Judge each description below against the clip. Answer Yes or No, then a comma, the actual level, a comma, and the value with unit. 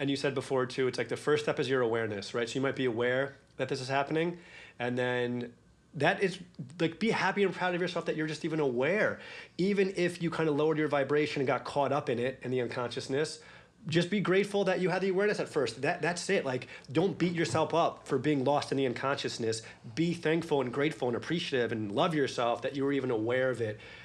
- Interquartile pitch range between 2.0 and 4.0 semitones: No, average, 4.5 semitones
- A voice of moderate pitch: Yes, medium, 145 Hz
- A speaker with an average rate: No, fast, 240 wpm